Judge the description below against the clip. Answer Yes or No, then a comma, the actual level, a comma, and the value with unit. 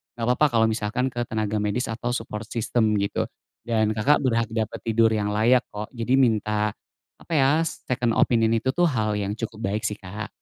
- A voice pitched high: No, low, 115 Hz